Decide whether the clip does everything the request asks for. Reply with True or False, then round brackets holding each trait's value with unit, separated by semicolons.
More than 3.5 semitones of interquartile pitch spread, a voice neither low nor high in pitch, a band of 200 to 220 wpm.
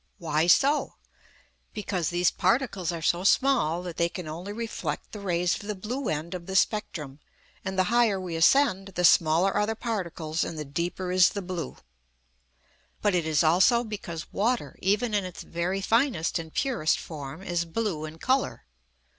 False (4.1 semitones; 180 Hz; 175 wpm)